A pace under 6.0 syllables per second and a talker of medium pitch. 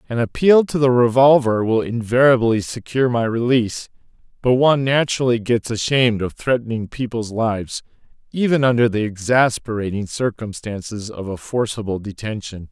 No: 5.3 syllables/s; low, 115 Hz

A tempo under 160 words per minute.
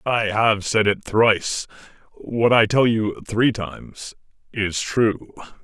Yes: average, 140 wpm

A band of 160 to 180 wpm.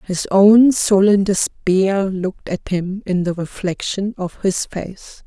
No: average, 150 wpm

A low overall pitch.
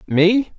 No: high, 200 Hz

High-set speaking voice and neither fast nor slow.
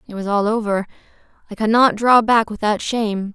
Yes: high, 215 Hz; average, 195 wpm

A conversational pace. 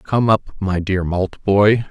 Yes: average, 155 wpm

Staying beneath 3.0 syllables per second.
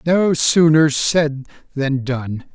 Yes: 2.8 syllables/s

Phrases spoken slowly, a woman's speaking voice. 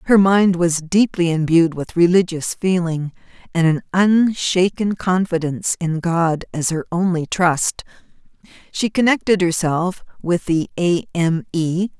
Yes: slow, 130 wpm; female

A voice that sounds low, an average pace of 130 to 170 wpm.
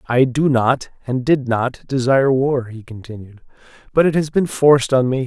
No: low, 130 Hz; average, 195 wpm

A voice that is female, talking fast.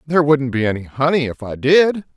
No: male; fast, 220 wpm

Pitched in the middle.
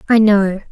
No: high, 205 Hz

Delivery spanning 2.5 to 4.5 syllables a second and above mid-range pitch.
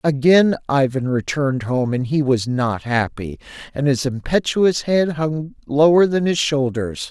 No: 4.2 syllables/s; medium, 140 Hz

